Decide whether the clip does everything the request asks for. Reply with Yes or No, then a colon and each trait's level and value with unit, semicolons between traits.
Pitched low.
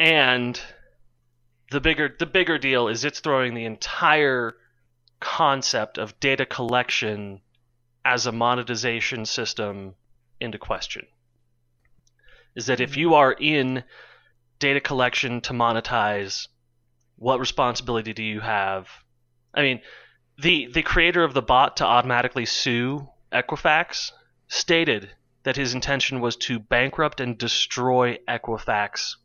Yes: low, 120 Hz